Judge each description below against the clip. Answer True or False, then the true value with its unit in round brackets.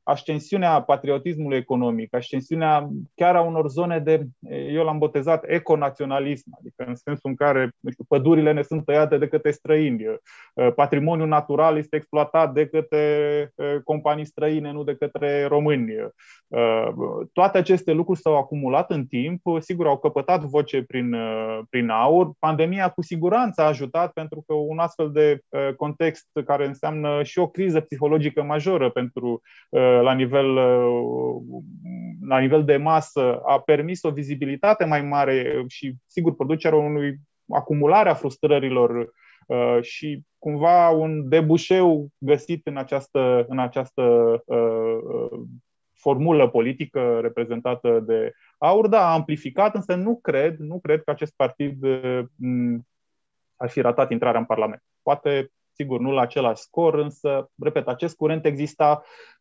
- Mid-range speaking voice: True (150 Hz)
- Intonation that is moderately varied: True (3.1 semitones)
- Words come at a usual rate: True (135 wpm)